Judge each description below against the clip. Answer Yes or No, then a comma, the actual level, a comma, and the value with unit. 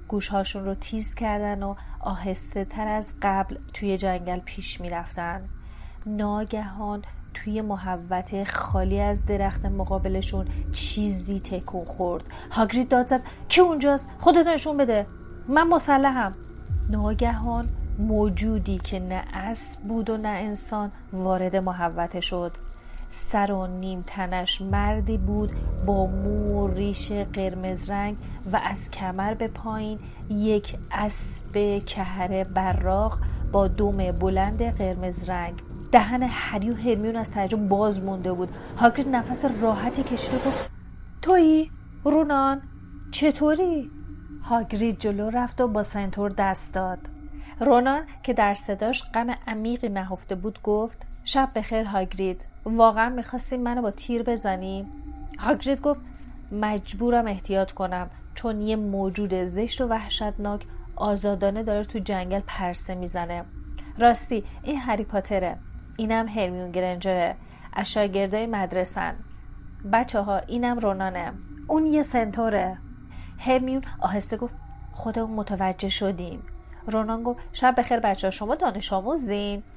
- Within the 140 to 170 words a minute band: No, average, 125 wpm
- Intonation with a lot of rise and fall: No, average, 3.6 semitones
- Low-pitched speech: No, high, 205 Hz